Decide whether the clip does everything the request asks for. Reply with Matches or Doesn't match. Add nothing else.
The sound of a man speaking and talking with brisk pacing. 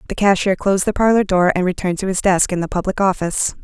Doesn't match